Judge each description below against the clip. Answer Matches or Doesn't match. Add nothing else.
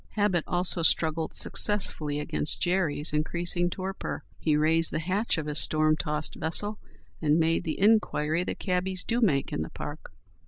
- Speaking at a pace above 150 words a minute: Matches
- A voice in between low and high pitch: Matches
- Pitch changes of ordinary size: Matches